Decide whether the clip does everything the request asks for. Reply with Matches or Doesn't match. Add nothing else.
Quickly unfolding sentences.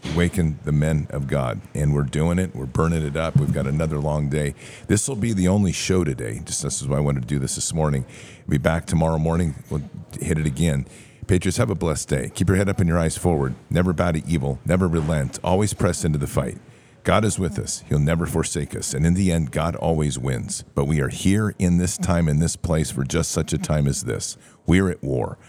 Matches